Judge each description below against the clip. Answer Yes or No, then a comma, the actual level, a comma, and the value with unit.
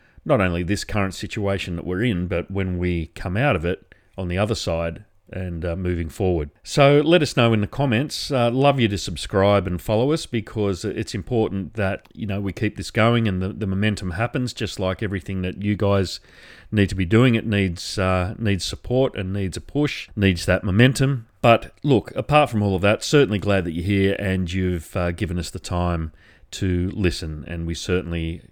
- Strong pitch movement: No, average, 3.6 semitones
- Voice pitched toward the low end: Yes, low, 100 Hz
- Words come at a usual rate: No, fast, 210 wpm